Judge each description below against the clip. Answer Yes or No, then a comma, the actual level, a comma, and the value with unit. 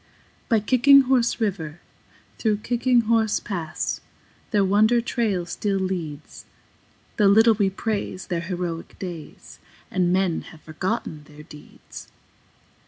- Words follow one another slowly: Yes, slow, 120 wpm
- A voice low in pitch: No, high, 195 Hz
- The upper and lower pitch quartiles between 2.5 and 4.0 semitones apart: No, average, 4.7 semitones